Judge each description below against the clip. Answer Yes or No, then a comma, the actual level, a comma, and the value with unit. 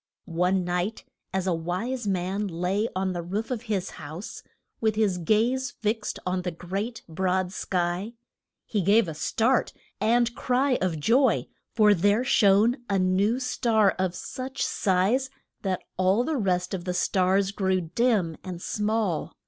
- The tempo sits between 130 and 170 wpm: Yes, average, 155 wpm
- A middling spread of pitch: Yes, average, 3.8 semitones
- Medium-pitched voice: No, high, 195 Hz